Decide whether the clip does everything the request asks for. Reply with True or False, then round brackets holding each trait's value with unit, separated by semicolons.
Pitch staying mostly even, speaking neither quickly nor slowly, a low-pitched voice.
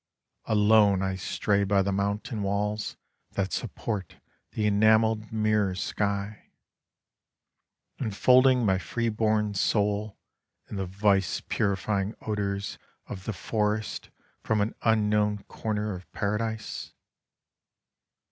False (1.5 semitones; 110 wpm; 105 Hz)